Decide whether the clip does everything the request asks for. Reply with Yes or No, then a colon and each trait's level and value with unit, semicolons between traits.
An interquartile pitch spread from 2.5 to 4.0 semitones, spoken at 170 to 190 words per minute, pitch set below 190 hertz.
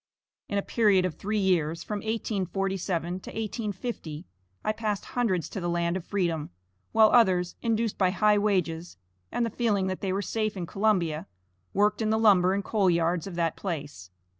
No: average, 3.5 semitones; average, 180 wpm; high, 195 Hz